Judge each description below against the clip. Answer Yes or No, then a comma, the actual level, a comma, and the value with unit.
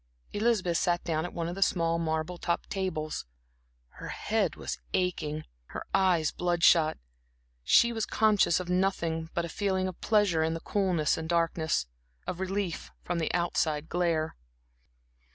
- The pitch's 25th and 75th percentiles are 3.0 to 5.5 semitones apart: No, narrow, 2.6 semitones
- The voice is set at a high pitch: No, medium, 170 Hz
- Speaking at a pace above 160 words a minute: No, average, 155 wpm